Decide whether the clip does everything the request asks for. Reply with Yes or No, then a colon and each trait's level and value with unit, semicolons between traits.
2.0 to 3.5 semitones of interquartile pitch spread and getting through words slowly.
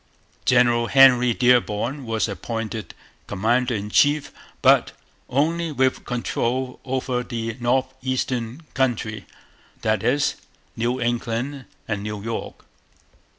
Yes: narrow, 2.5 semitones; slow, 110 wpm